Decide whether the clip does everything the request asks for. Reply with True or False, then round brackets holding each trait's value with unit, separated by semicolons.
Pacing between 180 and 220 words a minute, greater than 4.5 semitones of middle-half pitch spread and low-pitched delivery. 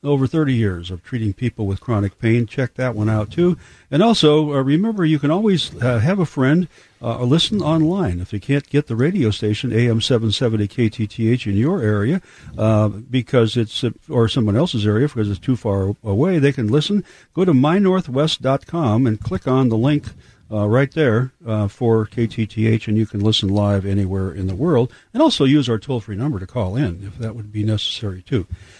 True (200 wpm; 5.2 semitones; 120 Hz)